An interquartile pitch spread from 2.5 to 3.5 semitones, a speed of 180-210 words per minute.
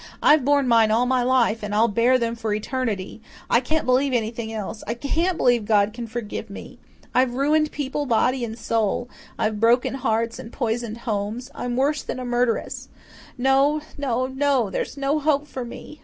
Yes: average, 3.0 semitones; average, 185 wpm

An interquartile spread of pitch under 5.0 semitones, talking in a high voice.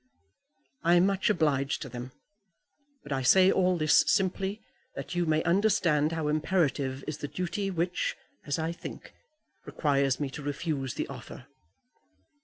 No: average, 4.3 semitones; medium, 160 Hz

